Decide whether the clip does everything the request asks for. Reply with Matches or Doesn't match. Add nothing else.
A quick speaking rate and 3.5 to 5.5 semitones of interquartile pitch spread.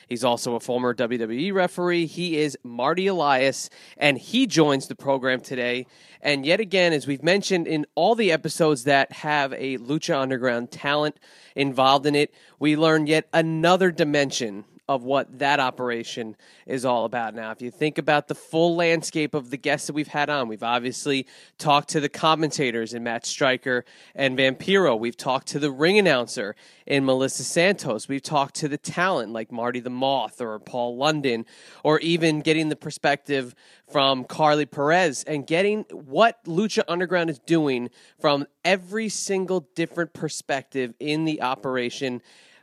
Doesn't match